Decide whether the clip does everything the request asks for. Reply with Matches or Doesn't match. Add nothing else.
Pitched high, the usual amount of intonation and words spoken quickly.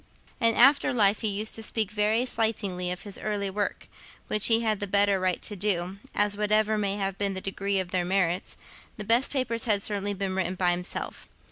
Doesn't match